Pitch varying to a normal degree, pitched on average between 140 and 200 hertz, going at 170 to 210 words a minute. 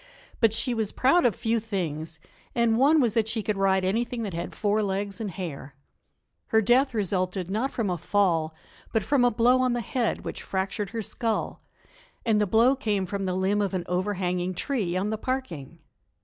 No: average, 3.8 semitones; high, 210 Hz; average, 195 wpm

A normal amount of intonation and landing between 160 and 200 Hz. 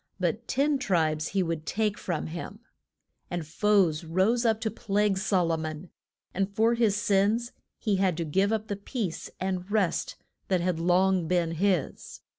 Yes: average, 3.6 semitones; high, 190 Hz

